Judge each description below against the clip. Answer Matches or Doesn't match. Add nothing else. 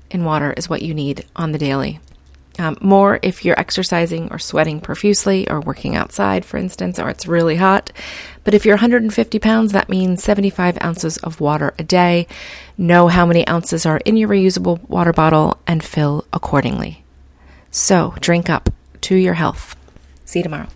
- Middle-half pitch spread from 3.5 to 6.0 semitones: Matches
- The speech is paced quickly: Doesn't match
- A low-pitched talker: Doesn't match